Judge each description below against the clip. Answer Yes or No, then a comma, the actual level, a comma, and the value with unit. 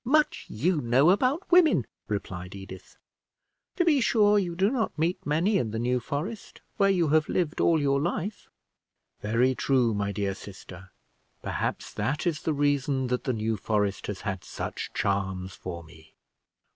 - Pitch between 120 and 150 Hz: Yes, low, 135 Hz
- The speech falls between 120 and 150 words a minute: No, average, 165 wpm